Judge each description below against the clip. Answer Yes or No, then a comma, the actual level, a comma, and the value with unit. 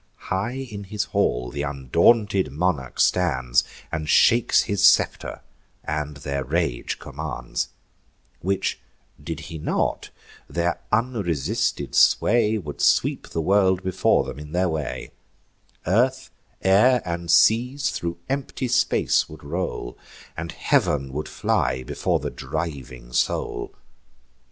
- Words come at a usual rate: No, slow, 120 wpm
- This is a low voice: Yes, very low, 85 Hz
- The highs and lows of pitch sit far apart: Yes, wide, 6.1 semitones